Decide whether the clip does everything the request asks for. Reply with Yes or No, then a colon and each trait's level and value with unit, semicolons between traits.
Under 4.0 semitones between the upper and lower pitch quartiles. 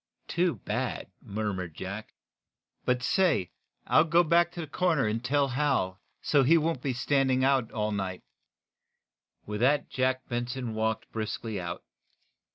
No: average, 5.3 semitones